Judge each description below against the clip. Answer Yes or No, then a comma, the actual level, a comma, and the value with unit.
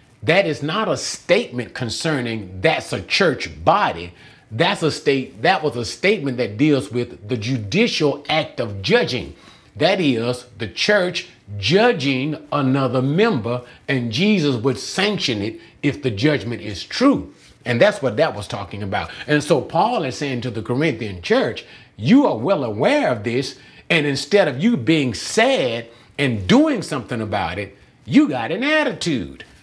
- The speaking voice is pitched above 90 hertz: Yes, low, 135 Hz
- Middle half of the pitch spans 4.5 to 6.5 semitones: Yes, average, 5.3 semitones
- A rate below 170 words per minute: Yes, average, 160 wpm